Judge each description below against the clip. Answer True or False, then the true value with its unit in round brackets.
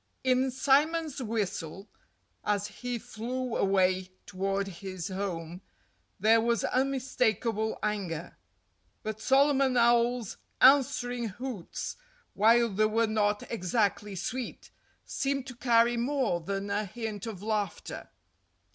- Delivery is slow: True (100 wpm)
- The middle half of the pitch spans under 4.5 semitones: True (4.1 semitones)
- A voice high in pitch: True (225 Hz)